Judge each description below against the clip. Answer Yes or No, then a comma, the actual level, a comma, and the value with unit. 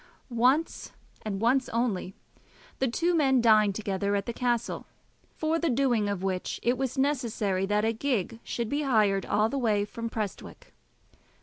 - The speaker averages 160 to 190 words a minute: Yes, average, 165 wpm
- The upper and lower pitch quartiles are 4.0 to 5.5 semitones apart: Yes, average, 4.5 semitones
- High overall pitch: Yes, high, 230 Hz